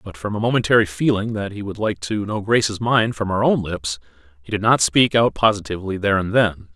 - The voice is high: No, low, 105 Hz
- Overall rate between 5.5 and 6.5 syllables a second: Yes, 5.8 syllables/s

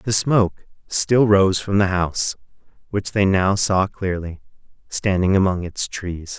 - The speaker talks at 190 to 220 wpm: No, average, 150 wpm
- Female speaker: No, male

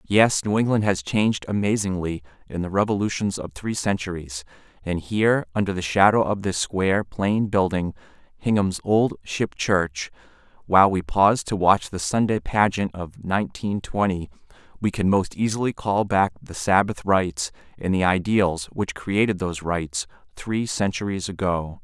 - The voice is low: Yes, very low, 95 Hz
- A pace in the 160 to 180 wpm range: No, average, 150 wpm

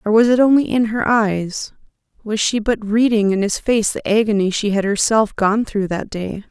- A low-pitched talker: No, high, 215 Hz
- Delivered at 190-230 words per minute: Yes, fast, 205 wpm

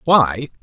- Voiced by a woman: No, male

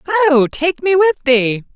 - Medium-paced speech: Yes, average, 170 wpm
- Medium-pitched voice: No, very high, 310 Hz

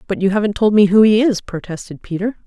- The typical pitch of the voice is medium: No, high, 200 Hz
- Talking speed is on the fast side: Yes, fast, 245 wpm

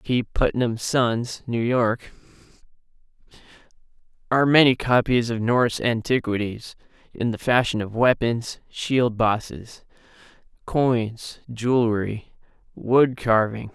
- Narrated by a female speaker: No, male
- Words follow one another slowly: Yes, slow, 95 wpm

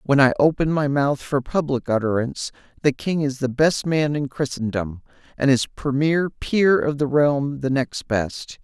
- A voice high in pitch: No, medium, 140 Hz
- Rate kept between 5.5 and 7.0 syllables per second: No, 4.5 syllables/s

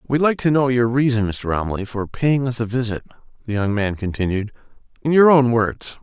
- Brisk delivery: Yes, fast, 210 wpm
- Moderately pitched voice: No, low, 120 Hz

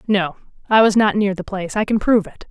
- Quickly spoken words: Yes, fast, 265 wpm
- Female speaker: Yes, female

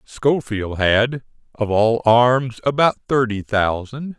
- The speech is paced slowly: Yes, slow, 115 wpm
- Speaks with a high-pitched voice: No, low, 120 Hz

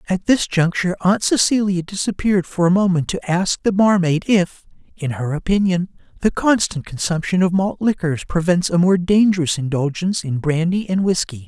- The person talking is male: Yes, male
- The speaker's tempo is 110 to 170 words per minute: Yes, average, 165 wpm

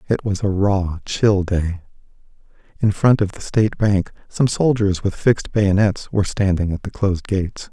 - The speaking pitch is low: Yes, low, 100 Hz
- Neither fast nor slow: Yes, average, 180 wpm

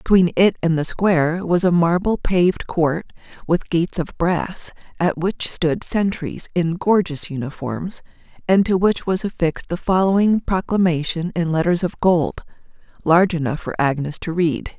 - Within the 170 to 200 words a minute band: No, average, 160 wpm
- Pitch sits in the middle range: Yes, medium, 175 Hz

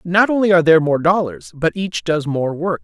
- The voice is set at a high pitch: No, medium, 165 Hz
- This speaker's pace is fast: Yes, fast, 230 wpm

